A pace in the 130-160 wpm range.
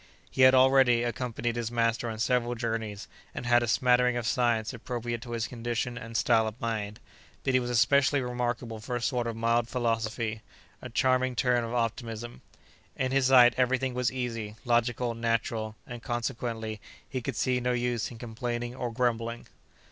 No: average, 180 wpm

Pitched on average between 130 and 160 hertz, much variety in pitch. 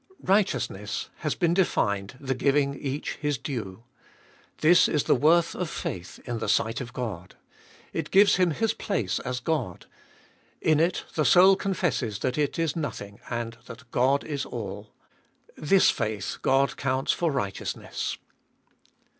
Yes: low, 135 Hz; wide, 6.1 semitones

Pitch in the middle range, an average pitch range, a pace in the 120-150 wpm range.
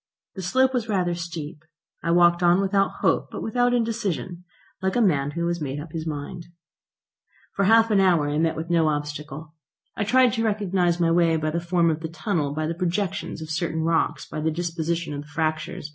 No: medium, 170 Hz; average, 3.5 semitones; fast, 205 wpm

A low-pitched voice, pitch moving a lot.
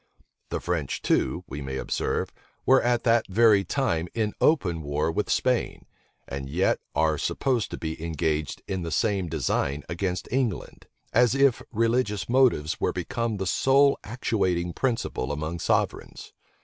Yes: very low, 95 Hz; wide, 6.7 semitones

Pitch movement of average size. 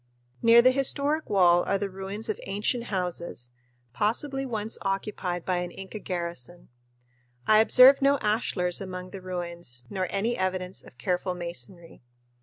Yes: average, 3.7 semitones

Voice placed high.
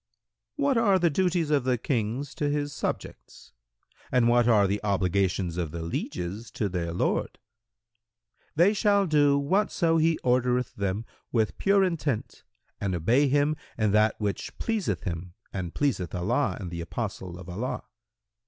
No: low, 115 Hz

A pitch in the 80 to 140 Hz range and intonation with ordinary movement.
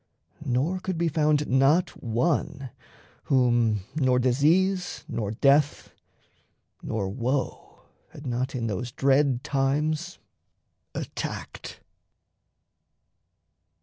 Yes: low, 135 Hz; average, 3.7 semitones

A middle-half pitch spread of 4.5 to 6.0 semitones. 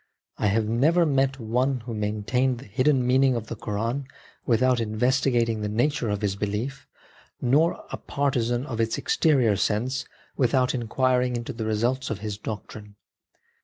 No: average, 3.3 semitones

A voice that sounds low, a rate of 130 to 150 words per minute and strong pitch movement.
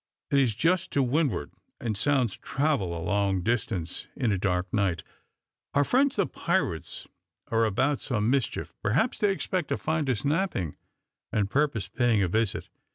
No: low, 120 Hz; average, 160 wpm; wide, 6.8 semitones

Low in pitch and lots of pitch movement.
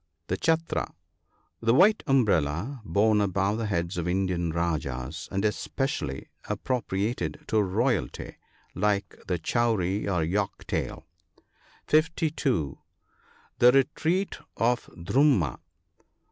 Yes: low, 105 Hz; wide, 6.6 semitones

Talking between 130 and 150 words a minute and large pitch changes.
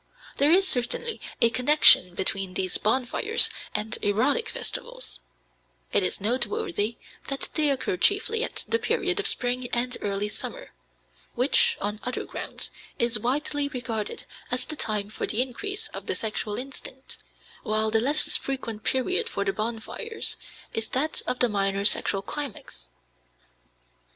Yes: average, 145 wpm; wide, 5.7 semitones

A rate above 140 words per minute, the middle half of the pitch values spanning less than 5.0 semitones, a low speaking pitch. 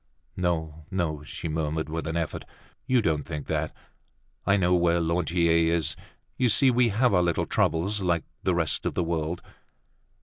Yes: average, 170 wpm; narrow, 2.5 semitones; very low, 85 Hz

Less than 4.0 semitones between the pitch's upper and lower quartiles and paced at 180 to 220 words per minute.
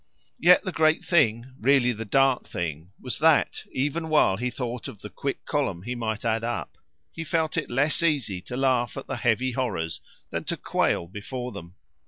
No: average, 4.6 semitones; average, 190 wpm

